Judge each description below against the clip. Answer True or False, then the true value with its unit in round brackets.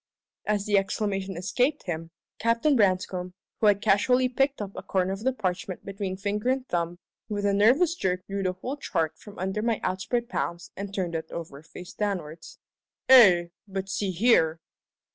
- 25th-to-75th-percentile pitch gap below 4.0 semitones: True (3.6 semitones)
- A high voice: True (195 Hz)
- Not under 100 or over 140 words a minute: False (175 wpm)